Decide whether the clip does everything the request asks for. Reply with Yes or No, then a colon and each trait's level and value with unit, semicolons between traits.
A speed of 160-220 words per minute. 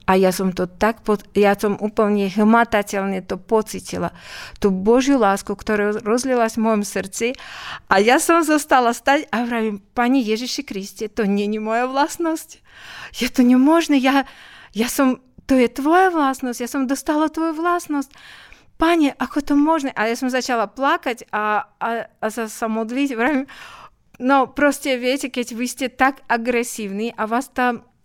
Yes: fast, 165 wpm